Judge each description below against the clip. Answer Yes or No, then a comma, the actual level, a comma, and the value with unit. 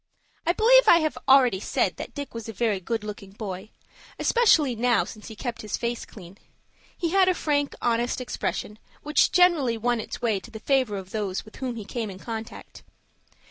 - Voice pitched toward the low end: No, high, 235 Hz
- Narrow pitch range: No, average, 5.0 semitones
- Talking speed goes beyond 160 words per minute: Yes, average, 195 wpm